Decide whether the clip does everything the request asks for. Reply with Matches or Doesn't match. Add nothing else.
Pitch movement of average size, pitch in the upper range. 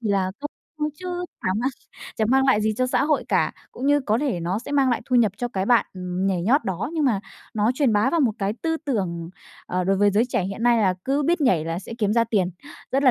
Doesn't match